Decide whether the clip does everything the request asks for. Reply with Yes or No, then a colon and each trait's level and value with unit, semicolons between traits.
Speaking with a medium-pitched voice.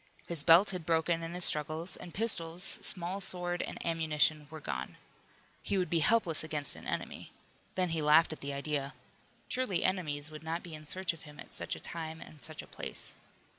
Yes: medium, 165 Hz